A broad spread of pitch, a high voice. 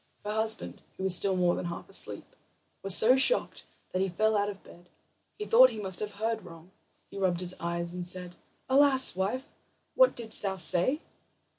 No: average, 3.9 semitones; high, 195 Hz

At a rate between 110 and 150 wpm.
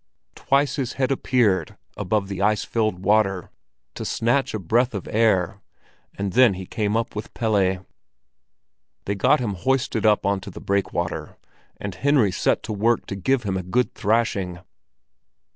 No: average, 160 wpm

